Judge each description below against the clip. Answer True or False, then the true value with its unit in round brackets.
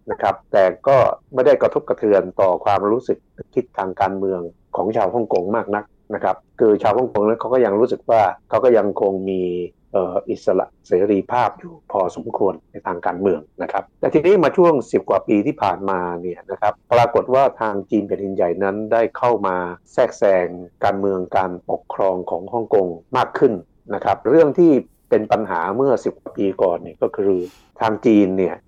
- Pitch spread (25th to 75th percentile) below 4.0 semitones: True (2.7 semitones)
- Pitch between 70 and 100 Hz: True (95 Hz)